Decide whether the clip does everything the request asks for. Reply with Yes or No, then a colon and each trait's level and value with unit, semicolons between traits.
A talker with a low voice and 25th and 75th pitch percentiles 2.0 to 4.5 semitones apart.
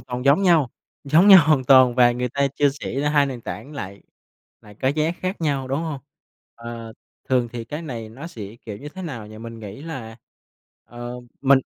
Yes: low, 130 Hz; average, 4.1 semitones